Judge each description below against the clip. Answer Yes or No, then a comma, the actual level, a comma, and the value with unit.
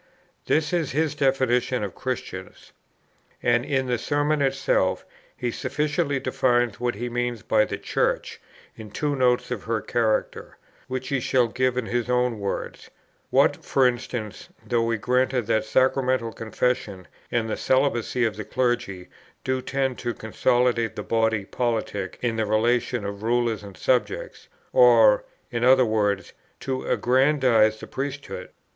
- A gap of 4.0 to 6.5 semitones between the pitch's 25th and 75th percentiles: No, average, 2.7 semitones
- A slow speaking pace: No, average, 150 wpm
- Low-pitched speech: Yes, low, 120 Hz